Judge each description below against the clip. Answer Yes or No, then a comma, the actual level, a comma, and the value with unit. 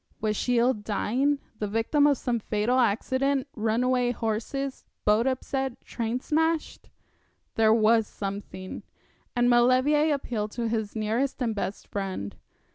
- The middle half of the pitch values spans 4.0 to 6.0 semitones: No, average, 3.4 semitones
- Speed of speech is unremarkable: No, slow, 130 wpm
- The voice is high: Yes, high, 235 Hz